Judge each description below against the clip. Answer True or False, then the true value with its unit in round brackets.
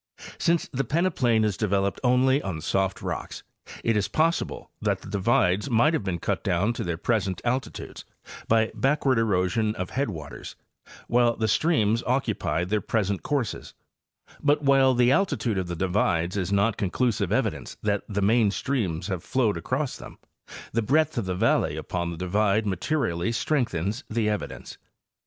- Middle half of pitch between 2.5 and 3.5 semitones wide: False (5.1 semitones)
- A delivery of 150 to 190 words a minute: True (160 wpm)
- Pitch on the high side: False (110 Hz)